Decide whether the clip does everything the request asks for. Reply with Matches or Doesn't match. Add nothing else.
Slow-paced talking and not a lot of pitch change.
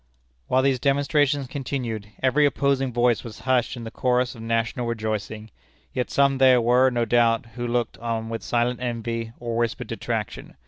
Doesn't match